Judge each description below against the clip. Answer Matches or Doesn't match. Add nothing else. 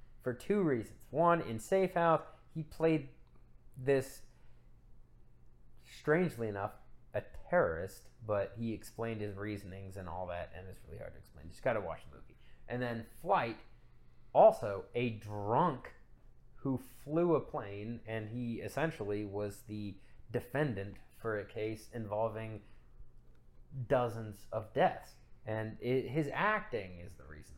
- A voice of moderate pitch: Doesn't match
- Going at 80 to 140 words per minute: Matches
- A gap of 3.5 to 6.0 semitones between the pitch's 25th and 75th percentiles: Matches